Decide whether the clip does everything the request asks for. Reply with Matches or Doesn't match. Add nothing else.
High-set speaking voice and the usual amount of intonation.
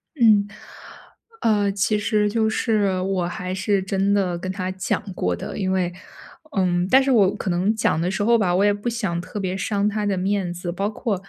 Doesn't match